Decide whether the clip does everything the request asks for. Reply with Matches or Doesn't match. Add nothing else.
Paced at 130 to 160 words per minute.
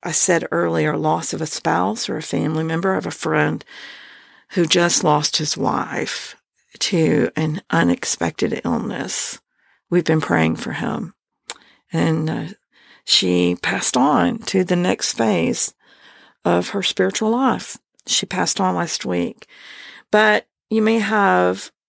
Matches